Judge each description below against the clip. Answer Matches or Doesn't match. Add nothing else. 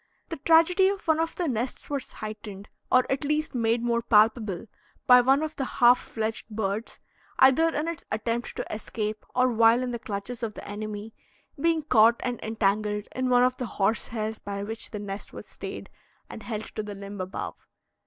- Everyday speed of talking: Matches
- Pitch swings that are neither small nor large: Matches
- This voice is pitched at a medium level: Doesn't match